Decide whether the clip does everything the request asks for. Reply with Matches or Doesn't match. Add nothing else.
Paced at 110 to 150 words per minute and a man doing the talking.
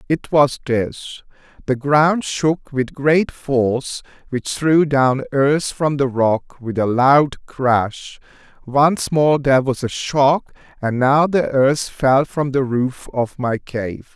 Matches